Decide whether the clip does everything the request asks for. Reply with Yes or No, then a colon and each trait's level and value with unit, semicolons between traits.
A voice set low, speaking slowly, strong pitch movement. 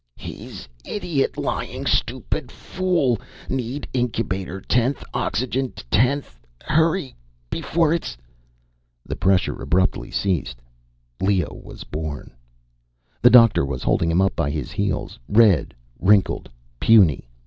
Yes: low, 105 Hz; slow, 115 wpm; wide, 6.9 semitones